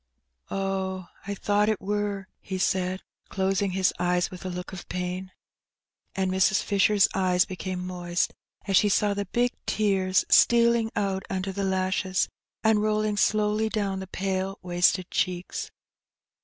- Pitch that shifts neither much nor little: No, narrow, 1.8 semitones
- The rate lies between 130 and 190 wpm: Yes, average, 145 wpm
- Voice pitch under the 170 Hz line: No, high, 190 Hz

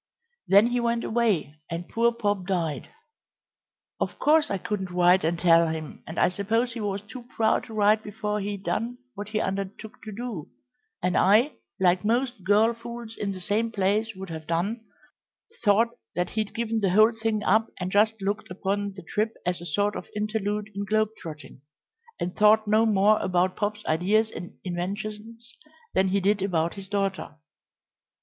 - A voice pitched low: No, high, 205 Hz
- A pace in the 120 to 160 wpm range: No, average, 175 wpm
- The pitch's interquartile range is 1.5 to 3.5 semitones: Yes, average, 2.9 semitones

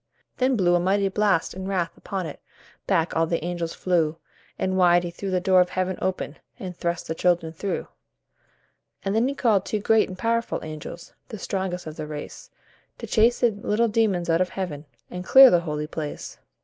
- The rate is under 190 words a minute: No, average, 200 wpm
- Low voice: No, medium, 185 Hz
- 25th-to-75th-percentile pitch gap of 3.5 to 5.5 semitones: No, average, 3.1 semitones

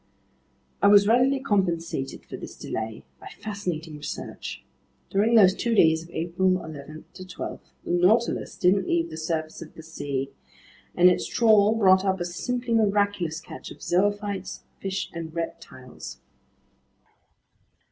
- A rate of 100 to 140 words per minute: Yes, slow, 135 wpm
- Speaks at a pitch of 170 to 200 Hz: Yes, medium, 185 Hz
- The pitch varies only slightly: No, average, 4.1 semitones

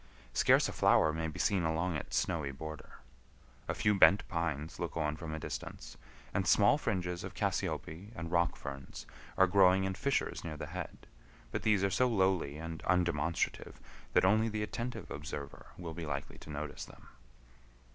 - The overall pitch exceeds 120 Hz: No, very low, 85 Hz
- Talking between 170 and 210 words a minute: Yes, average, 175 wpm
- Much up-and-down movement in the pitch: No, average, 3.7 semitones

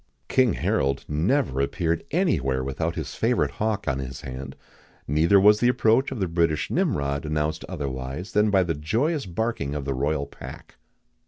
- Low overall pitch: Yes, very low, 80 Hz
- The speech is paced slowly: No, average, 175 wpm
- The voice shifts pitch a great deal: Yes, wide, 7.2 semitones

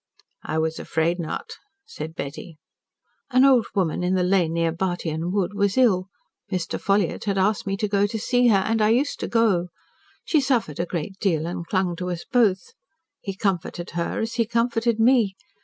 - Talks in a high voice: Yes, high, 195 Hz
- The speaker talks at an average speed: Yes, average, 190 wpm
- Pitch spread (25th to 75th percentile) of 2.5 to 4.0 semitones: No, average, 4.6 semitones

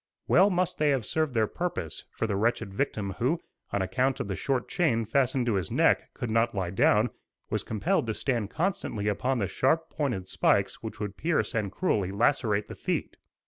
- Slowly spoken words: No, average, 195 wpm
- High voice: No, low, 115 Hz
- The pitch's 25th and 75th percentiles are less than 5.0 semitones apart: No, wide, 5.4 semitones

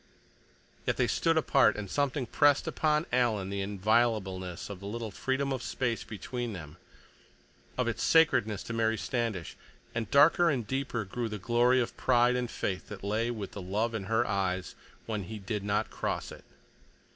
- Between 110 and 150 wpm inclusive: No, average, 175 wpm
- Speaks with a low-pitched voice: Yes, low, 115 Hz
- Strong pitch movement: No, average, 3.8 semitones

